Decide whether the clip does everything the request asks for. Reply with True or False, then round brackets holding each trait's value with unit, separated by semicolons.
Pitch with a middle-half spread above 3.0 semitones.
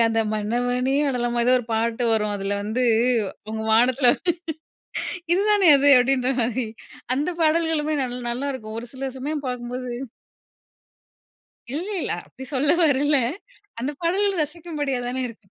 True (3.7 semitones)